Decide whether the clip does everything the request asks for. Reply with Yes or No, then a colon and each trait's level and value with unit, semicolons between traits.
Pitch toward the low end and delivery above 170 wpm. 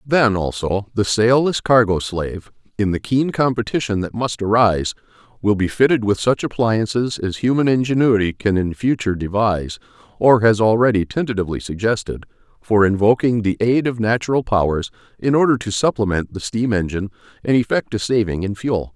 No: low, 110 Hz; average, 160 wpm